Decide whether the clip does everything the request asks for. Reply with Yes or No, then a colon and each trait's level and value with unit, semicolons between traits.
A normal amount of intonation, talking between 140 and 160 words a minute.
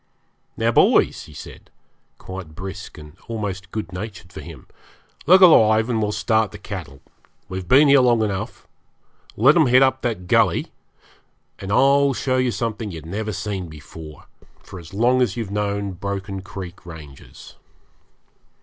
Yes: average, 4.0 semitones; average, 155 wpm